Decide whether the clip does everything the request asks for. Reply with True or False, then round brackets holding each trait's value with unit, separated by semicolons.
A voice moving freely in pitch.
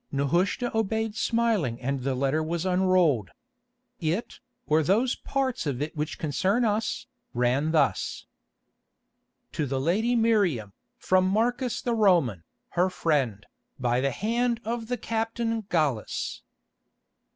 True (8.4 semitones)